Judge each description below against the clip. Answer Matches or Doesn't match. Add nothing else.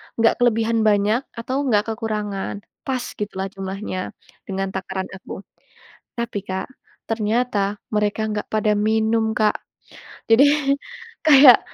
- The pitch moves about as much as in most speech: Doesn't match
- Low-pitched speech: Doesn't match